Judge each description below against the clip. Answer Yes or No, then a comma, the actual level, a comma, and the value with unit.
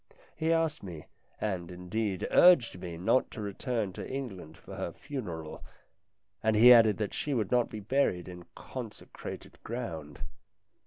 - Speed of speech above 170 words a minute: No, average, 150 wpm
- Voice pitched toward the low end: Yes, low, 105 Hz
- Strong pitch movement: Yes, wide, 5.9 semitones